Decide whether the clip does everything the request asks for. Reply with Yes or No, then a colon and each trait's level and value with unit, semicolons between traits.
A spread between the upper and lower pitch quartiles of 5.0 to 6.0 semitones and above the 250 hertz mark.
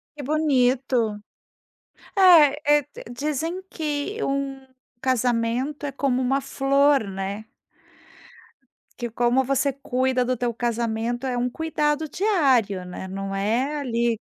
No: average, 3.5 semitones; very high, 260 Hz